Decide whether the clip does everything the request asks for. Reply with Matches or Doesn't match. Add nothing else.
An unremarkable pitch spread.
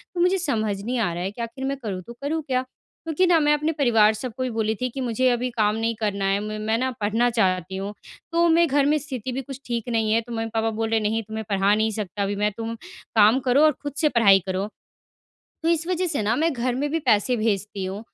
Matches